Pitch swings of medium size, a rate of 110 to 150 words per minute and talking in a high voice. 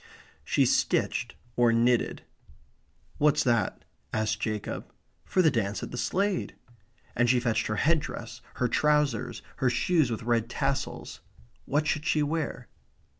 No: average, 4.4 semitones; average, 140 wpm; low, 125 Hz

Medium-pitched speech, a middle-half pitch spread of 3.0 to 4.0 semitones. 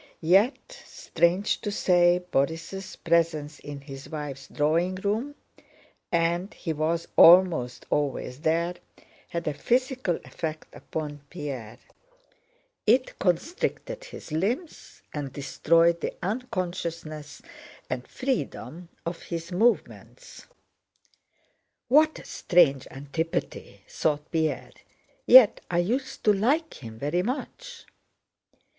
No: medium, 170 Hz; wide, 5.5 semitones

